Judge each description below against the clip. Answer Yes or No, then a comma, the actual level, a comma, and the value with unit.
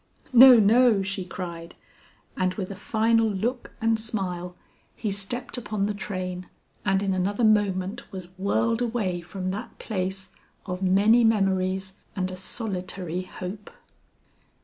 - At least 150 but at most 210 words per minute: No, slow, 135 wpm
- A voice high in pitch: Yes, high, 195 Hz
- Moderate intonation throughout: Yes, average, 3.0 semitones